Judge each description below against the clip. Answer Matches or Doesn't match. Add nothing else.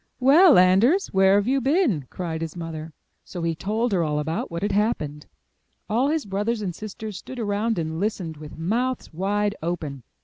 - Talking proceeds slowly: Doesn't match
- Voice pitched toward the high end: Matches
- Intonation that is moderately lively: Doesn't match